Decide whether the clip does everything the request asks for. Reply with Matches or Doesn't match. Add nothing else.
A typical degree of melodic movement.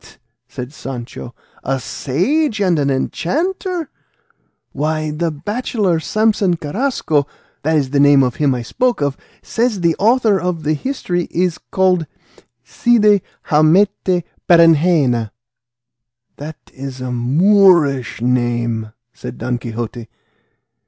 Doesn't match